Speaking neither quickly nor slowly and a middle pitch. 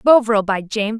No: average, 180 wpm; high, 220 Hz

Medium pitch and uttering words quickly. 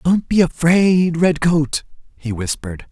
No: medium, 160 Hz; slow, 125 wpm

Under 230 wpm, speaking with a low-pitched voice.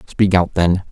Yes: average, 200 wpm; very low, 90 Hz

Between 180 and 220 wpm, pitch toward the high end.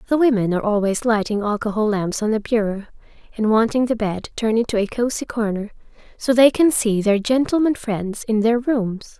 Yes: average, 190 wpm; high, 225 Hz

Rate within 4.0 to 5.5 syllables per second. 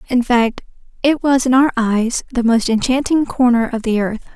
Yes: 4.8 syllables/s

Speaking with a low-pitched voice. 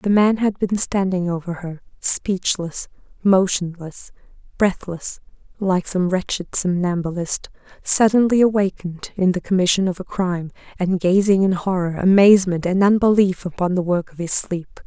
No: medium, 185 Hz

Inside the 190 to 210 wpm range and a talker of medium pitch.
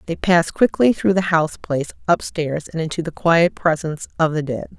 Yes: average, 200 wpm; medium, 165 Hz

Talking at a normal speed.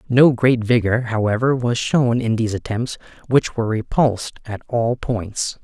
Yes: average, 160 wpm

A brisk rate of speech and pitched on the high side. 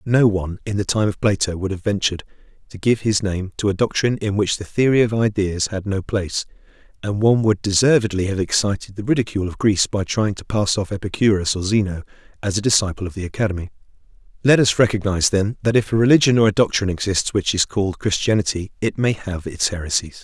No: fast, 210 wpm; low, 100 Hz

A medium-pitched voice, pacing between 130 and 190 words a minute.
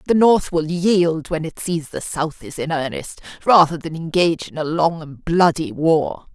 No: medium, 165 Hz; average, 200 wpm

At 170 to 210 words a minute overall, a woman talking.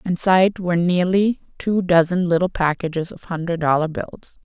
No: average, 150 wpm; female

